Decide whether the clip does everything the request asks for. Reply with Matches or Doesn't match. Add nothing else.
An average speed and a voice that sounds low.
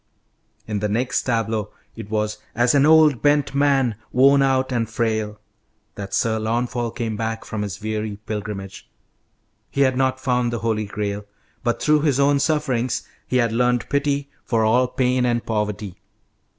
Matches